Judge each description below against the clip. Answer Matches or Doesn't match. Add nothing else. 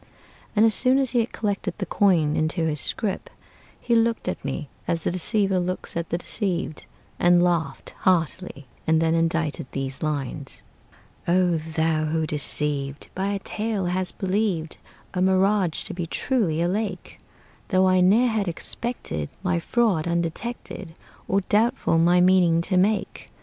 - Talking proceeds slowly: Doesn't match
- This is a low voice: Doesn't match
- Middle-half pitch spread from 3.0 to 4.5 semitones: Matches